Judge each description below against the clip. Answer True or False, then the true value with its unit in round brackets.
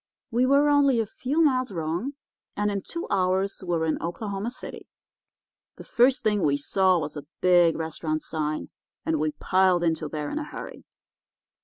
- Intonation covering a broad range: True (7.0 semitones)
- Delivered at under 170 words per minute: False (175 wpm)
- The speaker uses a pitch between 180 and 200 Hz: True (185 Hz)